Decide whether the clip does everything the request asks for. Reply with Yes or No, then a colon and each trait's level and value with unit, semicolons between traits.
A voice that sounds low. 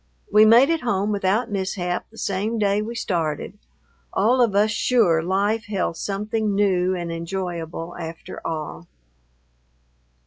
No: high, 195 Hz